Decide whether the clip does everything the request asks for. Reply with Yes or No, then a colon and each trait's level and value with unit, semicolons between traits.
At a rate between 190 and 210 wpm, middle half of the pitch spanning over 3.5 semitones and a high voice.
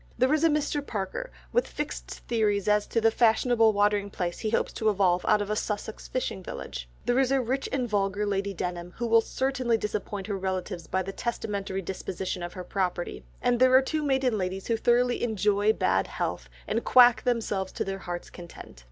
Yes: average, 200 wpm; average, 4.1 semitones; high, 210 Hz